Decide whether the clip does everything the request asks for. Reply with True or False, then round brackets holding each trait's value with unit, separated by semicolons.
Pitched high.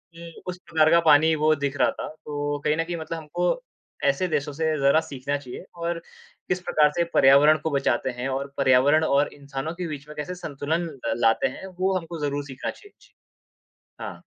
False (150 Hz)